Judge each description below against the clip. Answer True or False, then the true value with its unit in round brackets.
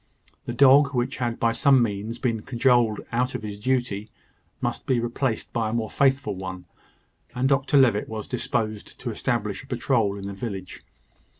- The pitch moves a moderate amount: True (3.5 semitones)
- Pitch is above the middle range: False (120 Hz)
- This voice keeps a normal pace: True (175 wpm)